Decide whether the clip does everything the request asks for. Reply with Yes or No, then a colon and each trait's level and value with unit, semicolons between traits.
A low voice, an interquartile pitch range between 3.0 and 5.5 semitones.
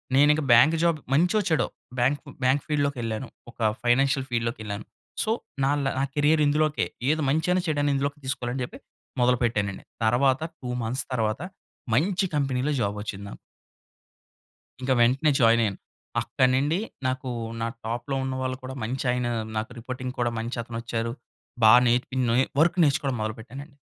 Yes: low, 130 Hz; average, 3.6 semitones